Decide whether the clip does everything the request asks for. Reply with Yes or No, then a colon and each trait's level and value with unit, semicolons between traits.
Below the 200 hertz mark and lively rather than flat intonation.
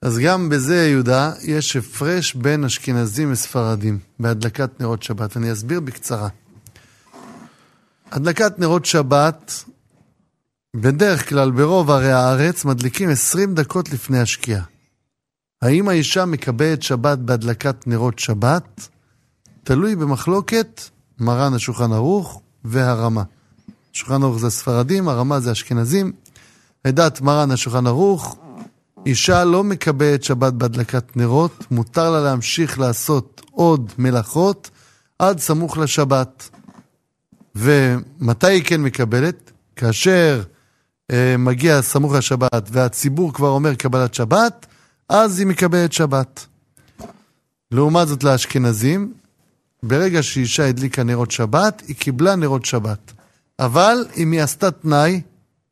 No: medium, 140 Hz; average, 4.8 semitones